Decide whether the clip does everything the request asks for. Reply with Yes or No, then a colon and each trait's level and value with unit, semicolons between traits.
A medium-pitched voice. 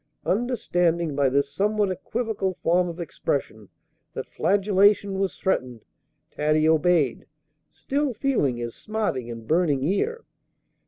Yes: medium, 175 Hz